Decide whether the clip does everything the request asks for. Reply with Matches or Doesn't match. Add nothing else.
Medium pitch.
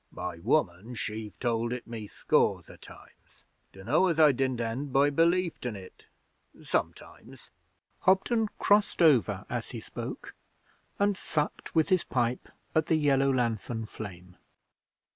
Doesn't match